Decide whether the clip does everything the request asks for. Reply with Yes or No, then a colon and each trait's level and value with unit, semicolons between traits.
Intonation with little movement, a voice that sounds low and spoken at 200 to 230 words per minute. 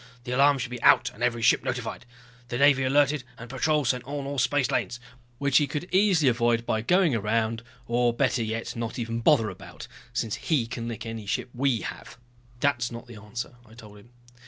No: average, 3.2 semitones; low, 120 Hz; fast, 205 wpm